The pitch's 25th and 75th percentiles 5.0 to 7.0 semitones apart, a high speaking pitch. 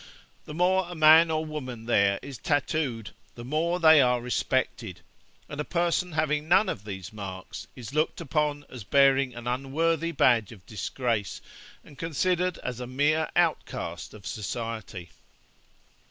No: wide, 5.5 semitones; low, 135 Hz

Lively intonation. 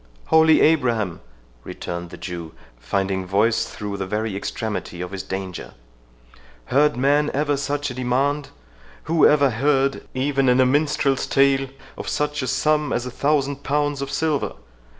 Yes: wide, 6.3 semitones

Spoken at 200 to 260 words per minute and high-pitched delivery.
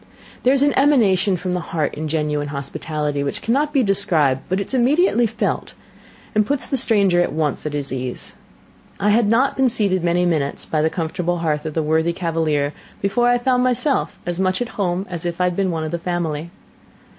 No: fast, 205 wpm; medium, 175 Hz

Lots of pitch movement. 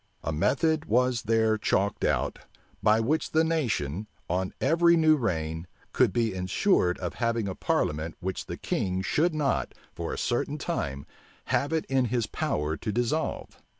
Yes: wide, 8.1 semitones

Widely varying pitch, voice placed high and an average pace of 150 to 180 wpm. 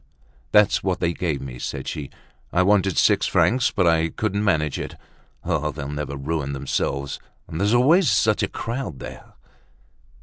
No: wide, 6.6 semitones; very low, 85 Hz; average, 165 wpm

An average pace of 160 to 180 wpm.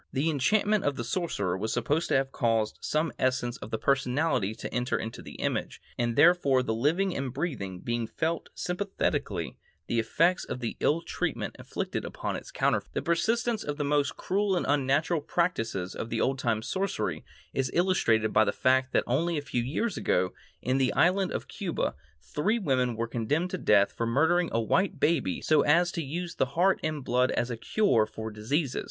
No: average, 190 wpm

